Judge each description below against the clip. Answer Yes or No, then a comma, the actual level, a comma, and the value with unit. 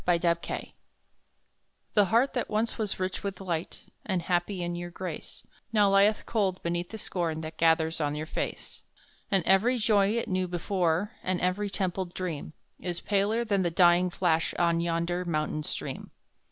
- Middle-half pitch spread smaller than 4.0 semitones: Yes, average, 2.8 semitones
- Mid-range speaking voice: Yes, medium, 180 Hz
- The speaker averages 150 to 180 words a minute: Yes, average, 165 wpm